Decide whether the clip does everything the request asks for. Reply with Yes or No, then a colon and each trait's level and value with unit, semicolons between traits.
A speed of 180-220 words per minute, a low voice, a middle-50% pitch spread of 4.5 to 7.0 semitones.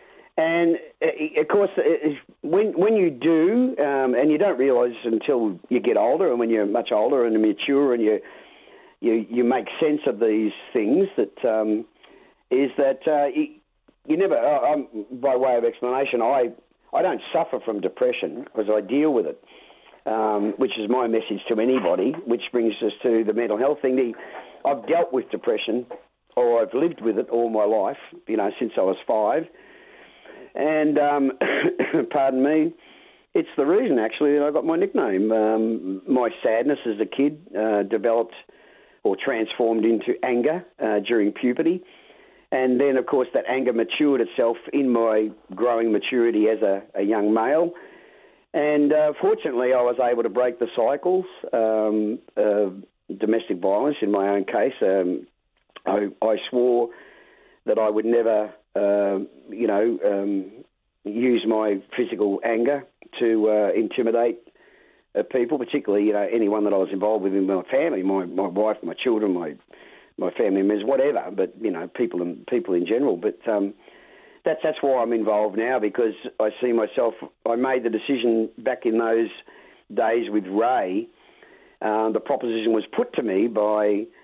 No: average, 165 wpm; low, 115 Hz; average, 5.2 semitones